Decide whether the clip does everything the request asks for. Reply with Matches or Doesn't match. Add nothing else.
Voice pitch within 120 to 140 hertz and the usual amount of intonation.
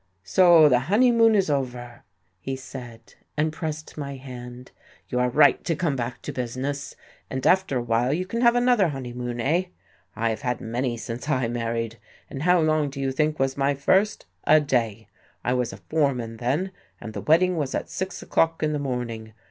Matches